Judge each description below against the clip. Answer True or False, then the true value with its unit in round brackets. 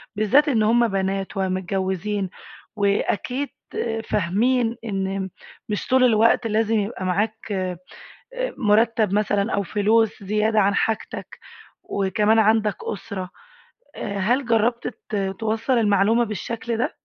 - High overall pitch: True (210 Hz)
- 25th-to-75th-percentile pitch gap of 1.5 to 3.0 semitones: True (2.5 semitones)